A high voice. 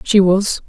Yes: high, 195 Hz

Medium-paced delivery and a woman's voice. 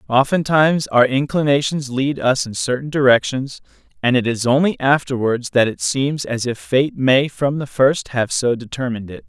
No: average, 175 wpm; male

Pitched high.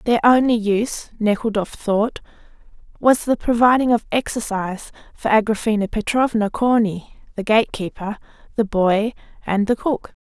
Yes: high, 220 Hz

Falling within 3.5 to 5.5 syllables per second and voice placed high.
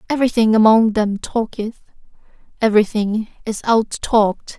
Yes: 5.1 syllables/s; high, 220 Hz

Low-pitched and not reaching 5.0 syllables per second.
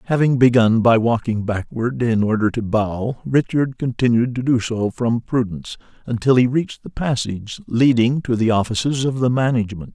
No: low, 120 Hz; 5.2 syllables/s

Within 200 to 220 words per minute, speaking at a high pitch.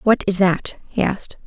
Yes: fast, 205 wpm; high, 195 Hz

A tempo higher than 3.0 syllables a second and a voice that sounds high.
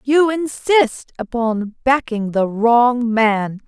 No: 2.9 syllables/s; high, 240 Hz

